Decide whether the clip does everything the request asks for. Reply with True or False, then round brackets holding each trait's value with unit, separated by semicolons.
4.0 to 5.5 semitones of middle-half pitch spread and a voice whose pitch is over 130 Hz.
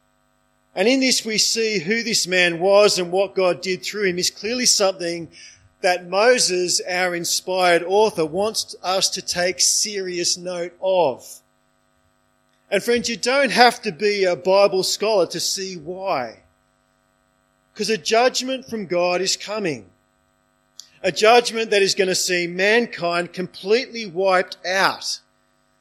False (3.4 semitones; 185 Hz)